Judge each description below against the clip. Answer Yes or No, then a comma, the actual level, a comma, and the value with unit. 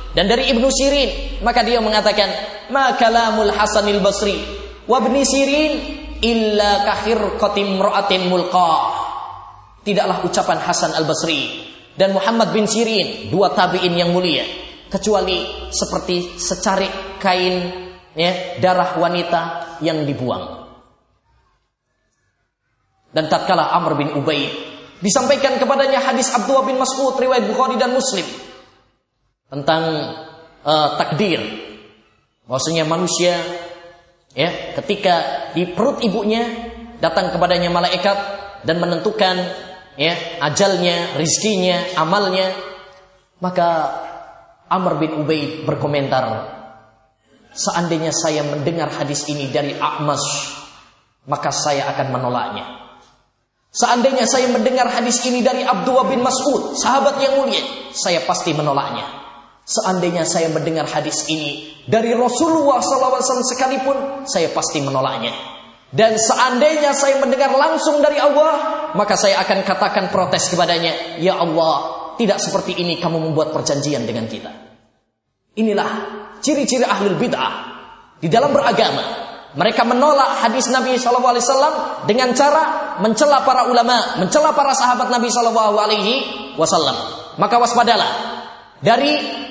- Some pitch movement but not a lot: No, wide, 7.4 semitones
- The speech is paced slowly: Yes, slow, 110 wpm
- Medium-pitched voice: No, high, 195 Hz